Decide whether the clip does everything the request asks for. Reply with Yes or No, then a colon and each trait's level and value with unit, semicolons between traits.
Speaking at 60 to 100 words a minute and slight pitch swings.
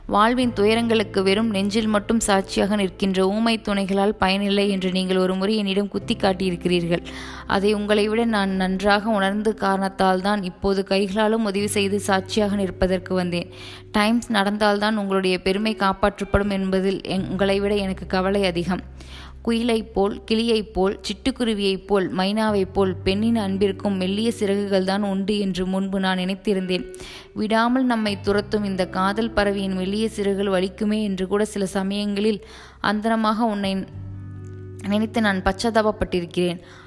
No: fast, 130 wpm; narrow, 1.9 semitones